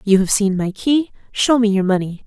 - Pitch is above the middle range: Yes, high, 210 Hz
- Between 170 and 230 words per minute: No, fast, 240 wpm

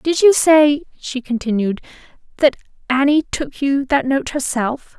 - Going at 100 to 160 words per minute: Yes, average, 145 wpm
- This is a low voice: No, very high, 275 Hz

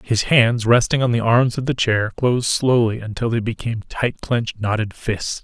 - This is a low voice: Yes, low, 115 Hz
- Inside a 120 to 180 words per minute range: No, average, 200 wpm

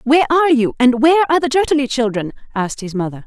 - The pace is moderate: No, fast, 220 wpm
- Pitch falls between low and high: No, very high, 265 Hz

